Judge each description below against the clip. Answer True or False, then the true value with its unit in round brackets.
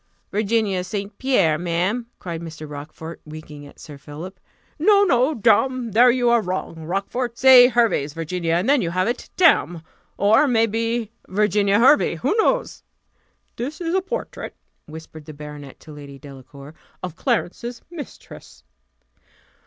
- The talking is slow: False (145 wpm)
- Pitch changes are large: True (7.2 semitones)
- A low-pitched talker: False (200 Hz)